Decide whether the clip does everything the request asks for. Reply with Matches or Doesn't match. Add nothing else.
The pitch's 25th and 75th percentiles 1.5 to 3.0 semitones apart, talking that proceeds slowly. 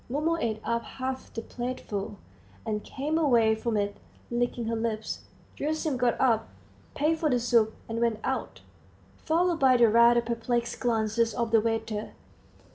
Doesn't match